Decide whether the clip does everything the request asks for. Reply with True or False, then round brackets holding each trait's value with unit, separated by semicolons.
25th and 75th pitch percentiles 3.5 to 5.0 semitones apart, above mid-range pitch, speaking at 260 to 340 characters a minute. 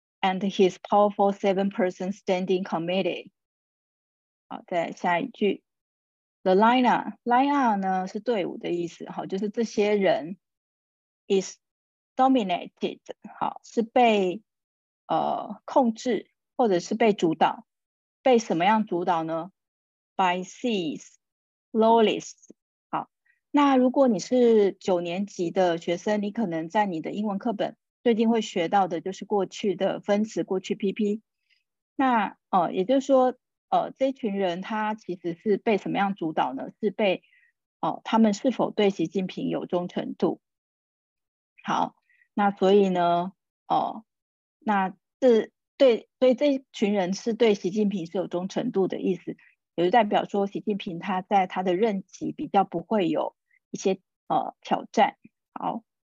True (3.9 semitones; 205 Hz; 265 characters per minute)